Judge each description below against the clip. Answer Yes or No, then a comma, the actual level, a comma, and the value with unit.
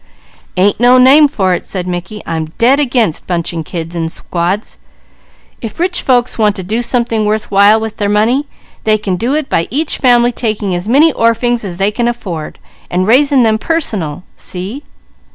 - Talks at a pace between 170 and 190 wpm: Yes, average, 180 wpm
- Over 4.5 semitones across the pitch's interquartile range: Yes, average, 5.0 semitones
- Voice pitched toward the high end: Yes, high, 215 Hz